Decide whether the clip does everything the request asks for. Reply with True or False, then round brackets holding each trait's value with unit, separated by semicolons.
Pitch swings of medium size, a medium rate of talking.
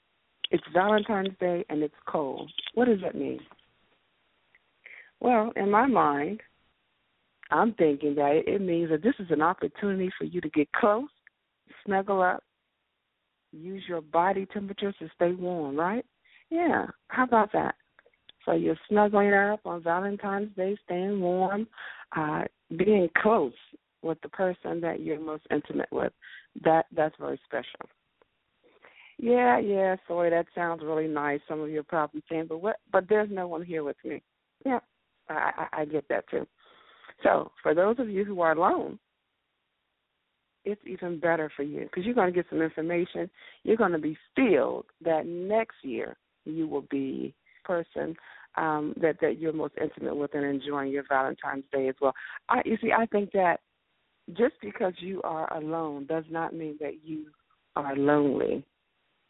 True (4.8 semitones; 160 wpm)